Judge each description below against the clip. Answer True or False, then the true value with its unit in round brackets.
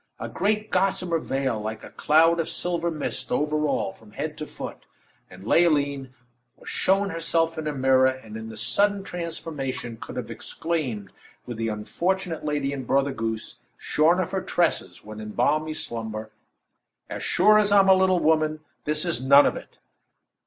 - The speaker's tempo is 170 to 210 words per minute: True (175 wpm)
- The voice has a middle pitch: True (150 Hz)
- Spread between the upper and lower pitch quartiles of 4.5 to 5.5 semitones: True (5.0 semitones)